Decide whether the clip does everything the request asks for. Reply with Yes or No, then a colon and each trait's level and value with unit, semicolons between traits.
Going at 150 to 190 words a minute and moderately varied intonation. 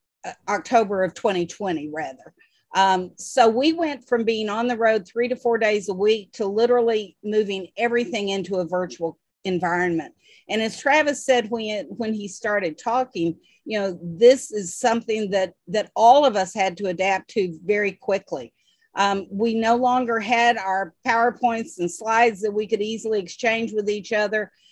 Yes: average, 165 wpm; average, 3.5 semitones